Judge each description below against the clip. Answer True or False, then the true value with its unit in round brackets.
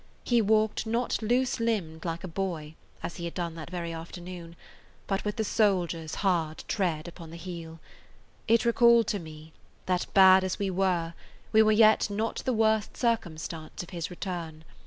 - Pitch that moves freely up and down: False (4.5 semitones)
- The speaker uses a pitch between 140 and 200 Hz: True (185 Hz)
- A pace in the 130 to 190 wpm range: True (175 wpm)